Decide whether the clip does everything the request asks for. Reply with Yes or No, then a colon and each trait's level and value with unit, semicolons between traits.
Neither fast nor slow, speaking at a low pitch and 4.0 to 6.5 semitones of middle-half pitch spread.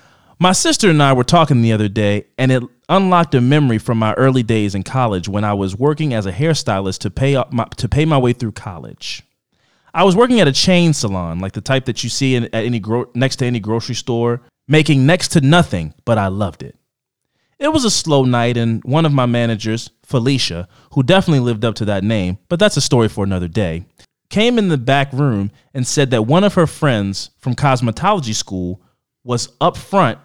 No: fast, 220 wpm; low, 125 Hz; average, 4.9 semitones